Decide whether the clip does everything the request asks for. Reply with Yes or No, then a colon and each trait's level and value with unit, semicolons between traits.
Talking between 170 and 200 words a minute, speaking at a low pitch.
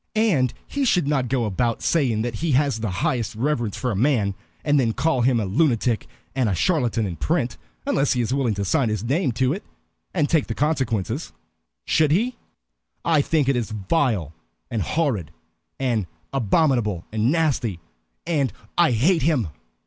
Yes: average, 175 wpm; low, 130 Hz